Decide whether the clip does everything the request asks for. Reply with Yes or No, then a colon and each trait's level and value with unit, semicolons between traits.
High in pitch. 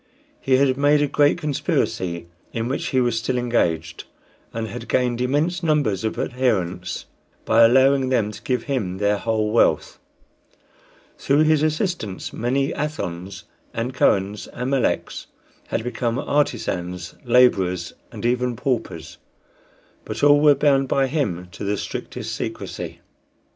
No: low, 125 Hz